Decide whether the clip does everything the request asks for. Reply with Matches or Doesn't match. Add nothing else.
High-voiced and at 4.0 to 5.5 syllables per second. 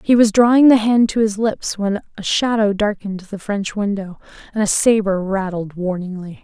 Matches